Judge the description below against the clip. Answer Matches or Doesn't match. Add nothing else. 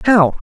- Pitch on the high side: Matches